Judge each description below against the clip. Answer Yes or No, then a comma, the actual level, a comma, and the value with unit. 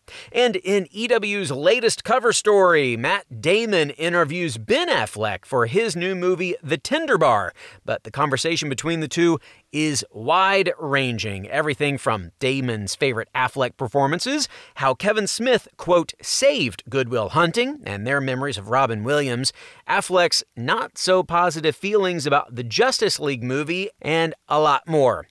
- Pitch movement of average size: No, wide, 6.0 semitones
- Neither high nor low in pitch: Yes, medium, 155 Hz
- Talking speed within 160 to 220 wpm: No, average, 140 wpm